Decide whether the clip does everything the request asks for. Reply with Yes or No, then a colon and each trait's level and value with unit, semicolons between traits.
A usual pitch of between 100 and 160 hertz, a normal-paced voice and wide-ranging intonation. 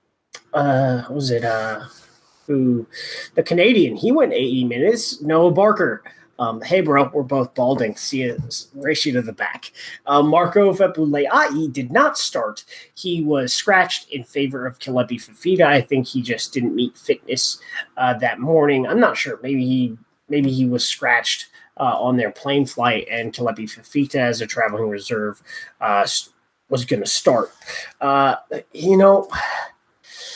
No: medium, 140 Hz; average, 155 wpm; average, 4.7 semitones